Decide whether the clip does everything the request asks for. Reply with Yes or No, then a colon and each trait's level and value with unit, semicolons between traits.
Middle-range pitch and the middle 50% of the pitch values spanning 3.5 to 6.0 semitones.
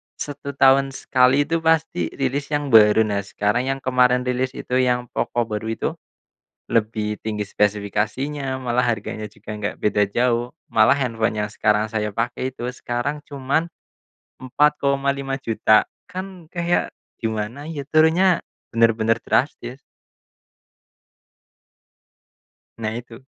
No: low, 125 Hz; average, 4.2 semitones